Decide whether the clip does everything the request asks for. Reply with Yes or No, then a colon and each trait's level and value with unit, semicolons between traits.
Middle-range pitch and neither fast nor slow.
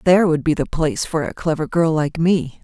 No: medium, 160 Hz; fast, 250 wpm